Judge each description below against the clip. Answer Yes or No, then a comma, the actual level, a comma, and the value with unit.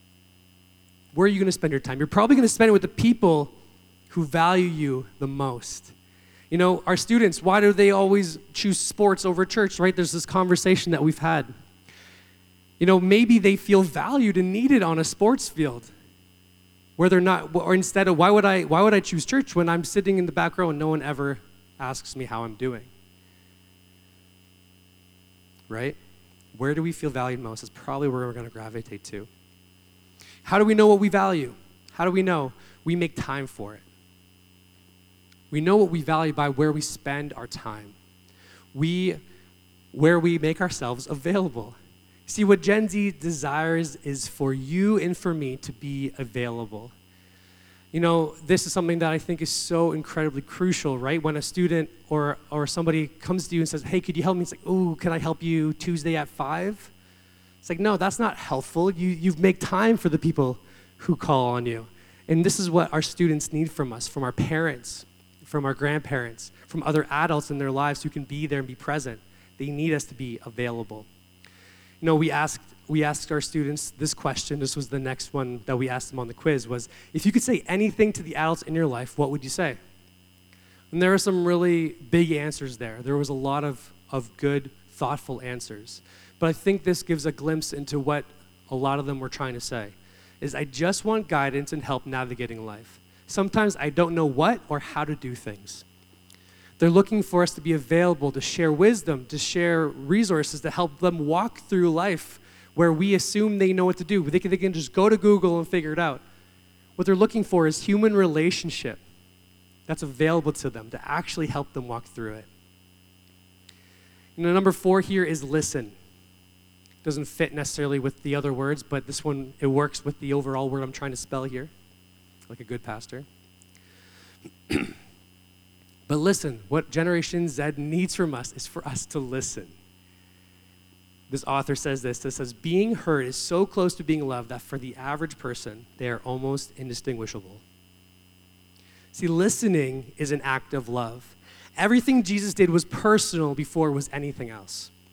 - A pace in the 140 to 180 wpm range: No, average, 190 wpm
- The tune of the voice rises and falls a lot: Yes, wide, 9.0 semitones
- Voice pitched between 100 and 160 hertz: Yes, medium, 140 Hz